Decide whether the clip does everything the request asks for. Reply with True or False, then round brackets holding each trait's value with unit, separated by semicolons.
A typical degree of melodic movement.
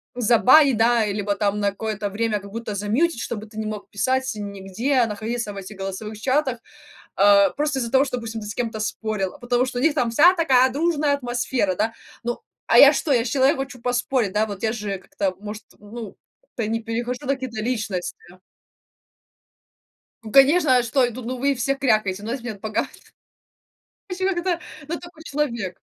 True (4.0 semitones)